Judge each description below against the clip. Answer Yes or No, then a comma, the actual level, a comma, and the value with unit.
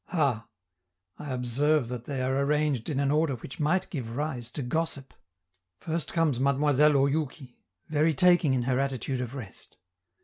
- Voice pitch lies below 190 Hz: Yes, medium, 140 Hz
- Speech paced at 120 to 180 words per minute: Yes, average, 160 wpm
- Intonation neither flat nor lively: Yes, average, 3.0 semitones